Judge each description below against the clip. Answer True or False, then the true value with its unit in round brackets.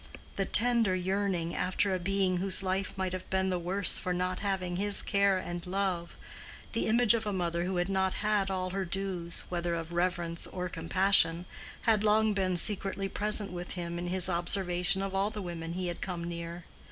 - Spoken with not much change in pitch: True (2.0 semitones)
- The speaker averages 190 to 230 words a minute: True (195 wpm)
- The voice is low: False (185 Hz)